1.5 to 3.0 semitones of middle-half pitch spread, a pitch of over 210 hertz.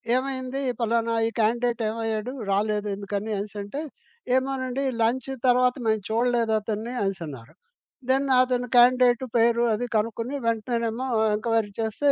Yes: narrow, 2.6 semitones; high, 230 Hz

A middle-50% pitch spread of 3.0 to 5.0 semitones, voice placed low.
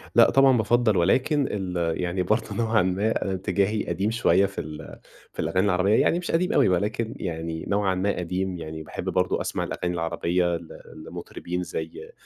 Yes: average, 3.9 semitones; very low, 95 Hz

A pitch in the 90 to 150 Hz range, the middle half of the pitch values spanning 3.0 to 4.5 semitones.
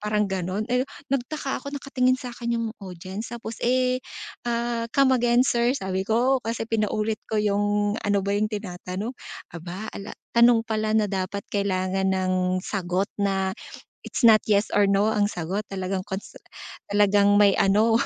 No: high, 210 Hz; average, 3.3 semitones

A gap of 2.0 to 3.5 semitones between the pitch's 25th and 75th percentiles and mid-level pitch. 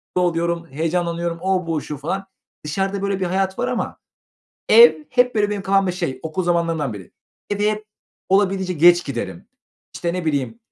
Yes: average, 2.8 semitones; medium, 180 Hz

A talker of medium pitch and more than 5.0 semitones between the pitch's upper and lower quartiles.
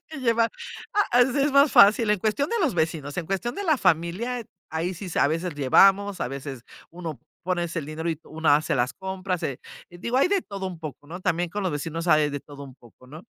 Yes: medium, 175 Hz; wide, 5.5 semitones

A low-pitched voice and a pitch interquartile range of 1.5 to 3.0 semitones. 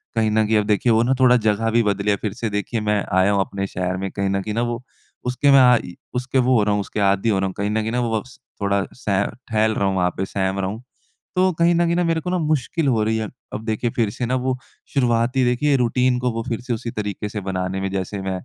No: low, 110 Hz; average, 3.7 semitones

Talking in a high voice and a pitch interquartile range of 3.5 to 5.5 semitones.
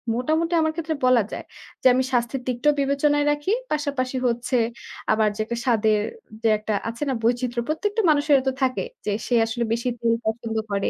Yes: very high, 255 Hz; average, 4.0 semitones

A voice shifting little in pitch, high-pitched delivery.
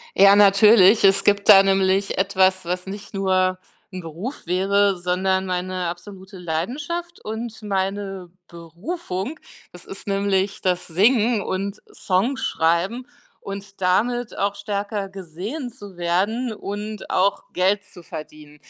Yes: narrow, 2.1 semitones; high, 195 Hz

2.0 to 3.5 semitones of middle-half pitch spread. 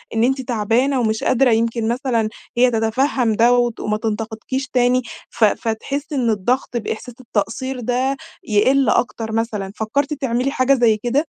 Yes: average, 2.8 semitones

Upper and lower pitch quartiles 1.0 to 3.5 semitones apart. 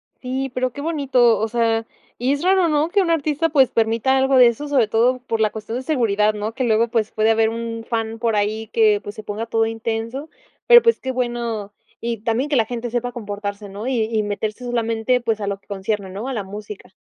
Yes: average, 3.0 semitones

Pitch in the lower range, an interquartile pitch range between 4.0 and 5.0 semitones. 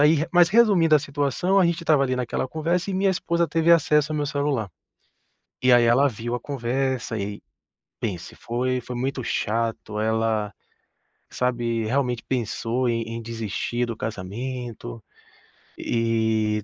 Yes: low, 125 Hz; average, 4.5 semitones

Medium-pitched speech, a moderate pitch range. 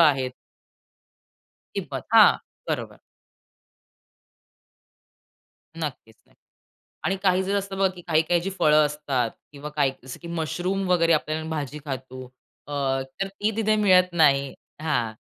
Yes: medium, 160 Hz; average, 4.3 semitones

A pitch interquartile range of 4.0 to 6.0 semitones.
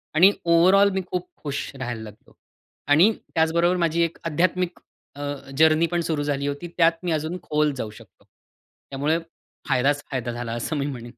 No: average, 3.5 semitones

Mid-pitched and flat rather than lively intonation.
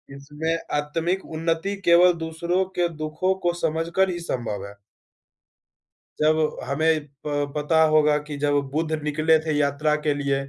Yes: medium, 155 Hz; narrow, 2.0 semitones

